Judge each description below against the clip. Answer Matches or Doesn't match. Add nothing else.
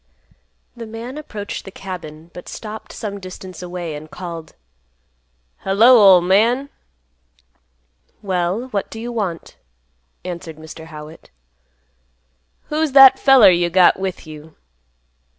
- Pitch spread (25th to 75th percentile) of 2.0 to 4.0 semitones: Doesn't match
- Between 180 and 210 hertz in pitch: Matches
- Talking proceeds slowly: Matches